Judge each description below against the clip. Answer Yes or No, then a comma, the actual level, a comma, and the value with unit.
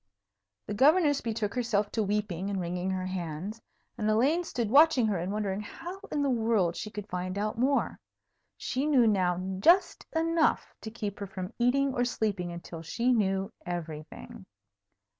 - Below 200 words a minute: Yes, average, 165 wpm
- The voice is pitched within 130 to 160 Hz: No, high, 210 Hz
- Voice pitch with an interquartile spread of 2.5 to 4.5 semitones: No, average, 4.9 semitones